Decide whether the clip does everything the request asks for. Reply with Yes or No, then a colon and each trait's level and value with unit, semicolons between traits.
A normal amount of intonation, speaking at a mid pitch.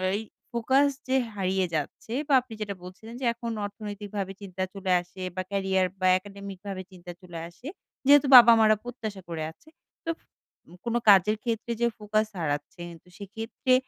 No: average, 3.6 semitones; high, 200 Hz